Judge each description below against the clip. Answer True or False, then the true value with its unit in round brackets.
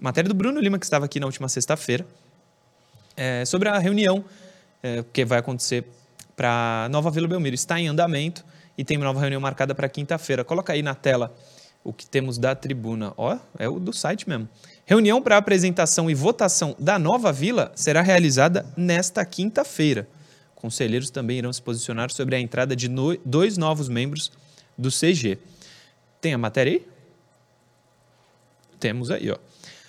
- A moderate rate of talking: True (160 wpm)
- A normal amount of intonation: False (5.7 semitones)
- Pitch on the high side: False (150 Hz)